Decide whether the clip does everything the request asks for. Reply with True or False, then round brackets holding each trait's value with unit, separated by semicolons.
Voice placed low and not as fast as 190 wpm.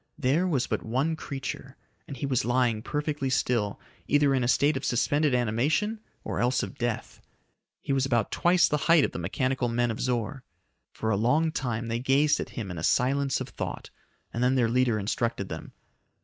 False (130 Hz; 195 wpm)